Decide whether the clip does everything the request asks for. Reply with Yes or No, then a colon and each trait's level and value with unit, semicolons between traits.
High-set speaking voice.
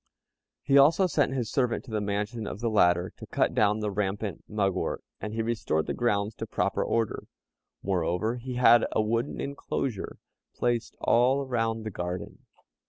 No: low, 110 Hz